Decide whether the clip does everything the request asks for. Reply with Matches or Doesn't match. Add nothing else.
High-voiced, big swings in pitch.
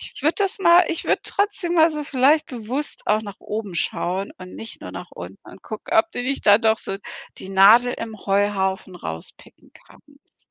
Matches